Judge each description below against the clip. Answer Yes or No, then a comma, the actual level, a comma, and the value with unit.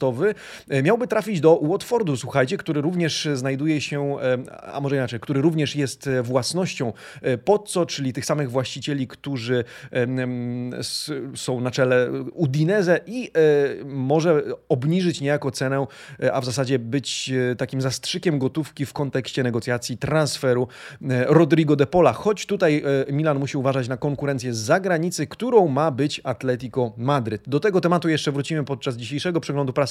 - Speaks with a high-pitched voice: No, medium, 140 Hz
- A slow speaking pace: No, average, 135 wpm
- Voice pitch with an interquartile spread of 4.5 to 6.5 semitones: No, average, 3.3 semitones